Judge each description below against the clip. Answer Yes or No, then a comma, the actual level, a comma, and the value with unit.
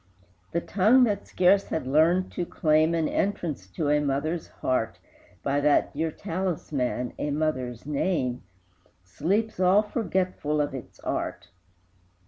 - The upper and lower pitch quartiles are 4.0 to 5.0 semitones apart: Yes, average, 4.7 semitones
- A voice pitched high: No, medium, 155 Hz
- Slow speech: Yes, slow, 130 wpm